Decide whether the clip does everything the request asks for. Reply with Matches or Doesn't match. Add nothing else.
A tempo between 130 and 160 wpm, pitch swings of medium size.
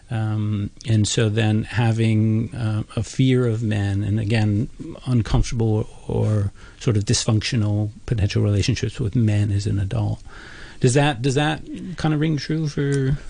Matches